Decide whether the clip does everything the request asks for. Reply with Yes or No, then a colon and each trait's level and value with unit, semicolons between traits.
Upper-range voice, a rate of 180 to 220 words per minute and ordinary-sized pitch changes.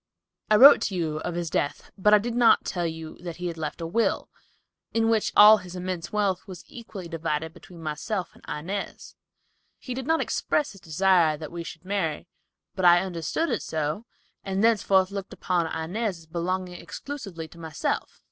No: medium, 180 Hz; average, 185 wpm; average, 4.0 semitones